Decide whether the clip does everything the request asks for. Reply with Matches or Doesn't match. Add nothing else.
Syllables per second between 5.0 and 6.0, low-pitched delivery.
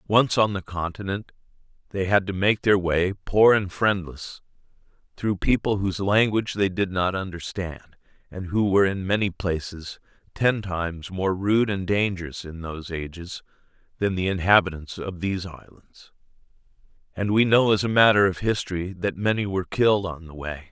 Matches